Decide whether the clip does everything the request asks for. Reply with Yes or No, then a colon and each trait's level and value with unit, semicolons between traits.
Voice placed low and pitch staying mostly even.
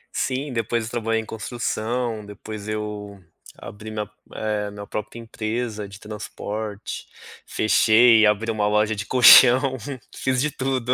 Yes: low, 110 Hz; narrow, 2.2 semitones